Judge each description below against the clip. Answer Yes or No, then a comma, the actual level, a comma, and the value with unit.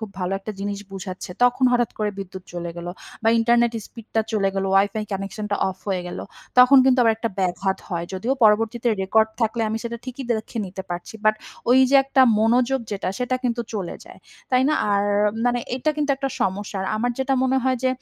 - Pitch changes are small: No, average, 4.2 semitones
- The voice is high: Yes, high, 220 Hz